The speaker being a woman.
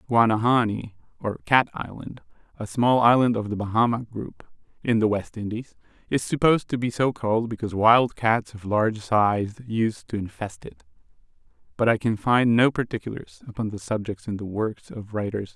No: male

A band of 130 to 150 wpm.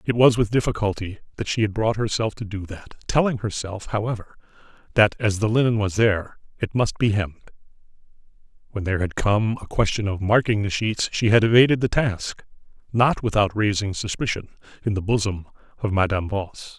No: average, 170 wpm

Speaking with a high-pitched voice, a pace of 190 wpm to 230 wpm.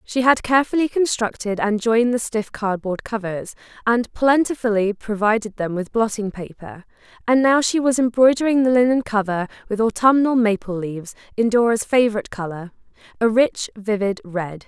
No: high, 220 Hz; average, 150 wpm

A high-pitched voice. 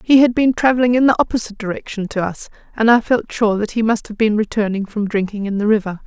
Yes: high, 220 Hz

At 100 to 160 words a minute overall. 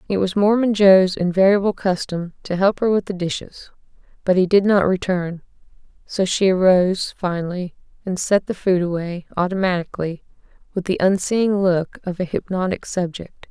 Yes: average, 155 wpm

